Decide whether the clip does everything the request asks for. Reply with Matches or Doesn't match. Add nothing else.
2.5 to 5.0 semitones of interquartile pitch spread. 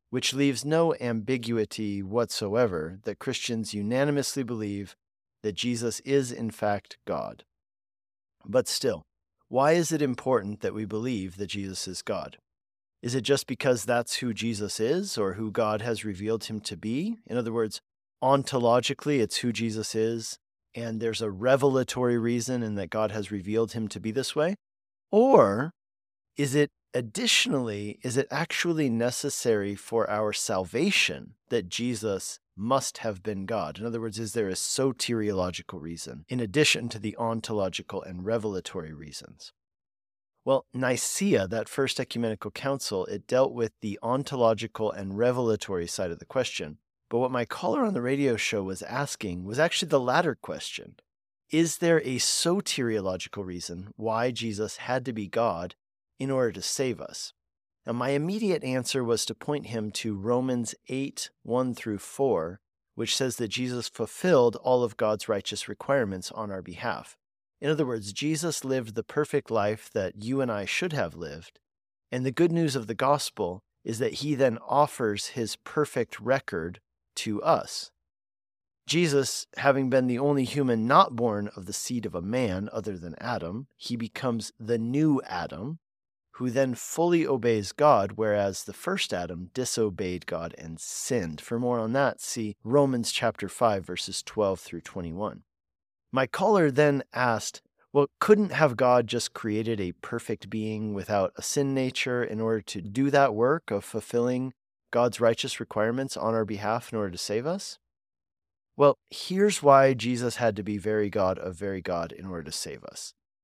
Matches